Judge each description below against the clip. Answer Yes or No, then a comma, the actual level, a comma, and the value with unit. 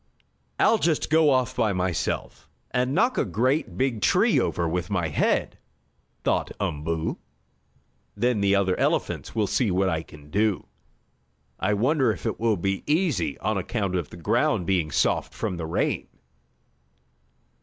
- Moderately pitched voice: No, low, 100 Hz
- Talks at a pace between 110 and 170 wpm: Yes, average, 155 wpm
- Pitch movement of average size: No, wide, 6.1 semitones